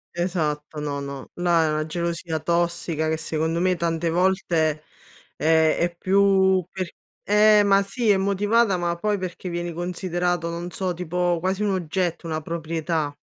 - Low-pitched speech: No, medium, 175 Hz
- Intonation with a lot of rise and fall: No, narrow, 2.6 semitones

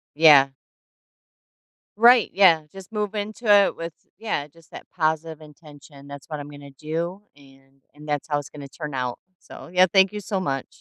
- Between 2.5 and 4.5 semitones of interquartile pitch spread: No, average, 5.0 semitones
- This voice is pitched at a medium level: Yes, medium, 155 Hz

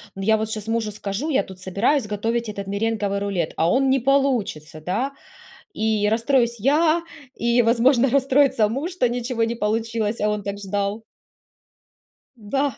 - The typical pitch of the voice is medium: No, high, 225 Hz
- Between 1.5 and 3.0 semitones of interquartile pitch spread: No, average, 4.0 semitones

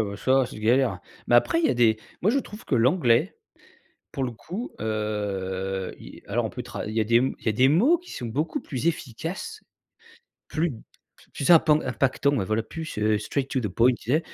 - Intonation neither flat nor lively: No, wide, 5.9 semitones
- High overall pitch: No, low, 125 Hz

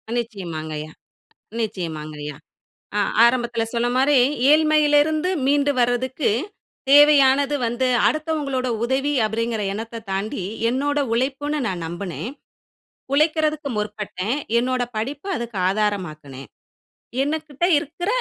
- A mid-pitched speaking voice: No, high, 245 Hz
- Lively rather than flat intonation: Yes, wide, 5.8 semitones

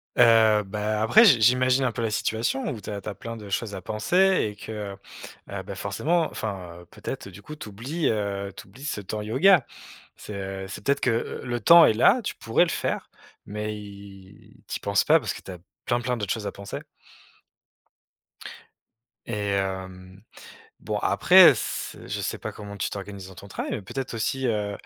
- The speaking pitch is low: Yes, low, 105 Hz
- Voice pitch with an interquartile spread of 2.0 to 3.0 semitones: No, average, 3.5 semitones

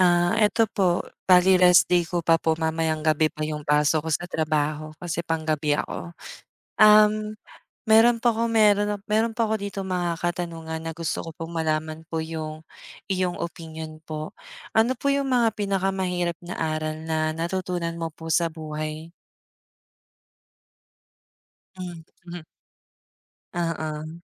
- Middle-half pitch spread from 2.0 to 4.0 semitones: Yes, average, 3.3 semitones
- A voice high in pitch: No, medium, 170 Hz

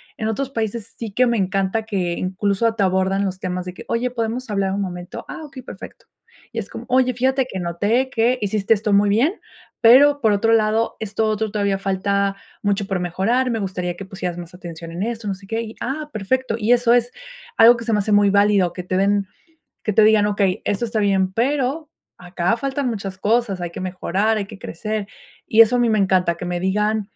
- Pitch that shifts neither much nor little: Yes, average, 3.3 semitones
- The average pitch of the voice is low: No, high, 210 Hz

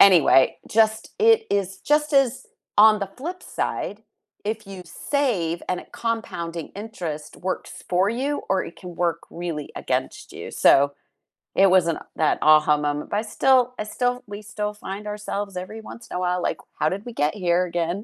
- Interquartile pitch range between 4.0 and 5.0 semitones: Yes, average, 4.5 semitones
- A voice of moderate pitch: No, high, 195 Hz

